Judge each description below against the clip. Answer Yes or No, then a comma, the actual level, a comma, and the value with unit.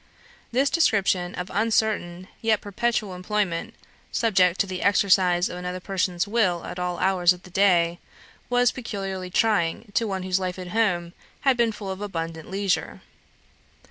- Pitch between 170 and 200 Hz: Yes, high, 190 Hz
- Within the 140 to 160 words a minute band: Yes, average, 155 wpm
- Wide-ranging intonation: No, average, 3.2 semitones